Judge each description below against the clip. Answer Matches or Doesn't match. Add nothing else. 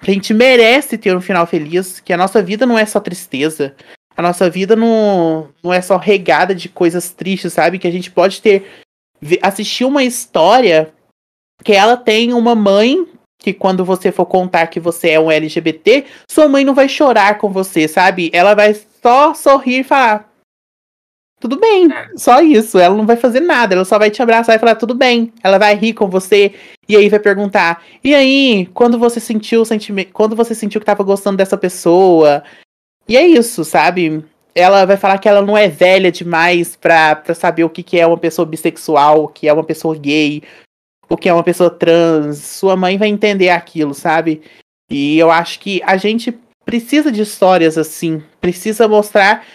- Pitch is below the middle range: Doesn't match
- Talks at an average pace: Doesn't match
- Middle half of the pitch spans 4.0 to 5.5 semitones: Matches